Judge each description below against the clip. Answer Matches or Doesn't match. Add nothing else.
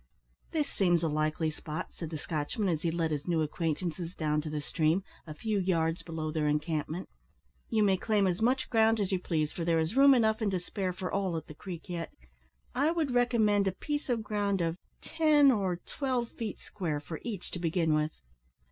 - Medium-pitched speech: Matches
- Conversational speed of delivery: Doesn't match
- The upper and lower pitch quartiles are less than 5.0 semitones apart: Doesn't match